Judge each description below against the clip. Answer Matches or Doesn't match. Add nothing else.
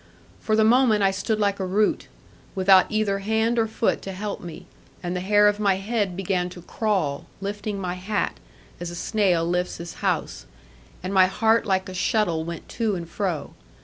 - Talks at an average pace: Matches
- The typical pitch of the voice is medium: Doesn't match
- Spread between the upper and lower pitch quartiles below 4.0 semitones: Matches